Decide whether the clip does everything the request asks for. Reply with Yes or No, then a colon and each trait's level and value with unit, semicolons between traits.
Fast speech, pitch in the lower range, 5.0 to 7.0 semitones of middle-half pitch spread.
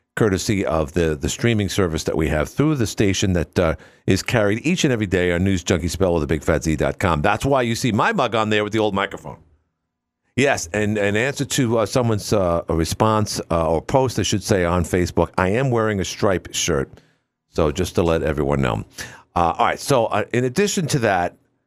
Yes: fast, 215 wpm; low, 100 Hz; wide, 5.4 semitones